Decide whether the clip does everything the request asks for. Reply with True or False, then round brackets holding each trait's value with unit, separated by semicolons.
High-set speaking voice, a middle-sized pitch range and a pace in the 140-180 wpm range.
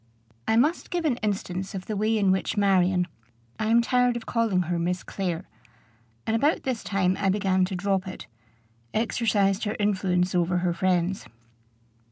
True (195 Hz; 3.4 semitones; 170 wpm)